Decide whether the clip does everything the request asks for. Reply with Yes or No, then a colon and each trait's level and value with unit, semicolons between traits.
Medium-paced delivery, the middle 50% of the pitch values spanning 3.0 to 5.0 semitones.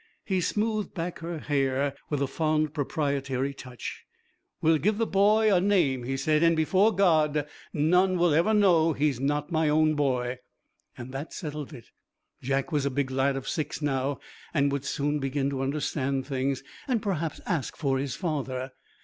Yes: average, 170 wpm; average, 3.5 semitones